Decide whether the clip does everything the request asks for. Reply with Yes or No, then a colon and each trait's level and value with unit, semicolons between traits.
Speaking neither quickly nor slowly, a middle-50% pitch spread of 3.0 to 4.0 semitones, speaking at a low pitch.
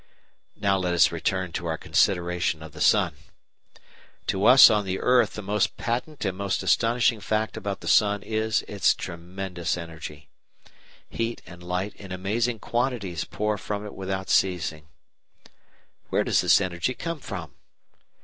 Yes: average, 160 wpm; average, 3.6 semitones; very low, 95 Hz